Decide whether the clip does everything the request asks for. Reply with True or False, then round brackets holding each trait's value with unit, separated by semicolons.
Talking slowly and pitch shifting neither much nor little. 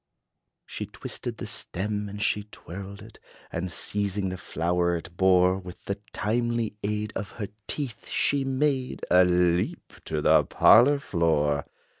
False (145 wpm; 3.3 semitones)